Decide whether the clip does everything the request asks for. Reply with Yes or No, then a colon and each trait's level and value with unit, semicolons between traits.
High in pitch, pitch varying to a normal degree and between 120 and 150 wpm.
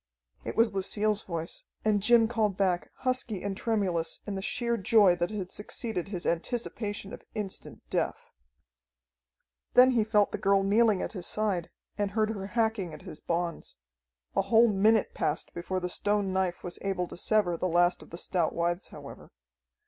No: high, 200 Hz; average, 3.3 semitones; average, 175 wpm